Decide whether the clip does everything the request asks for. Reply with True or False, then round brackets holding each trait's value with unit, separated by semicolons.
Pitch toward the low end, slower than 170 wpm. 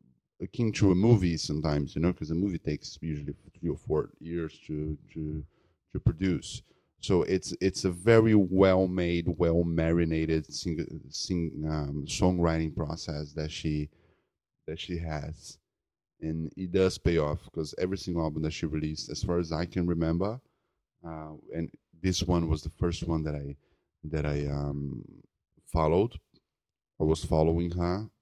True (85 Hz; 160 wpm)